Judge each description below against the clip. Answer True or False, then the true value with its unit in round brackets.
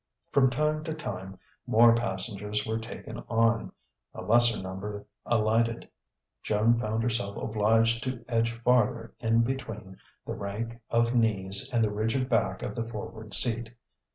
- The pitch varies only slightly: True (1.9 semitones)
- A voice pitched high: False (115 Hz)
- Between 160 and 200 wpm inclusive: False (145 wpm)